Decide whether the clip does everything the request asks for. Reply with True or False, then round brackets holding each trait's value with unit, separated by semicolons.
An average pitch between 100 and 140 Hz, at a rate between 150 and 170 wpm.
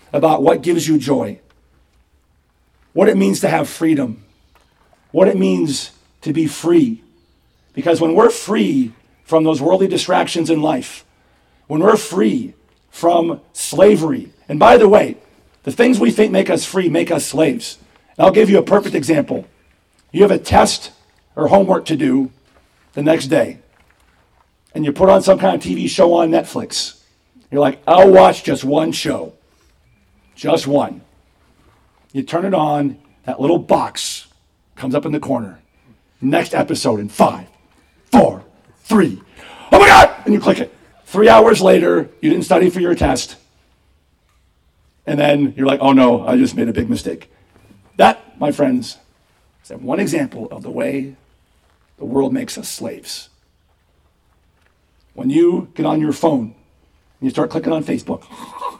True (135 Hz; 160 wpm)